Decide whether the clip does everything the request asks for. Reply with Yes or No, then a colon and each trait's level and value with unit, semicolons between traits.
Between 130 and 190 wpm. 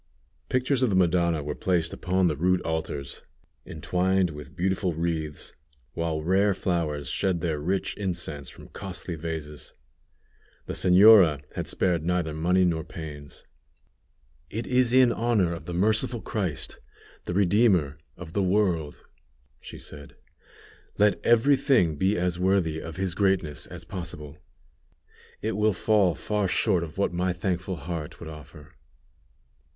Yes: average, 140 wpm